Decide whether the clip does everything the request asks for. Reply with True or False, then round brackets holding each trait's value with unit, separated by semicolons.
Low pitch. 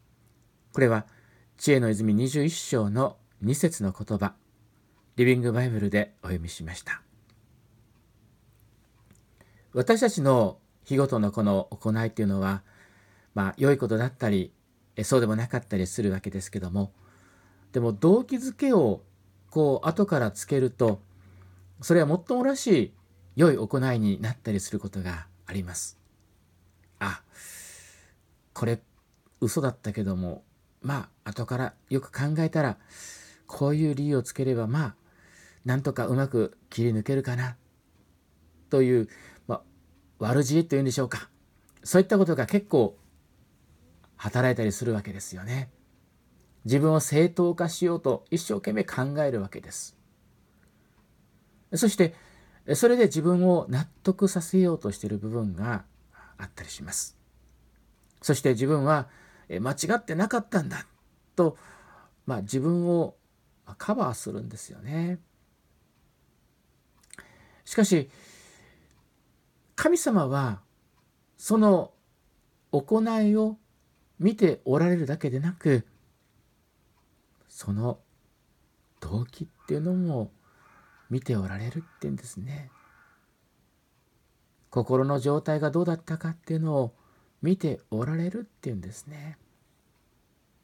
True (120 Hz)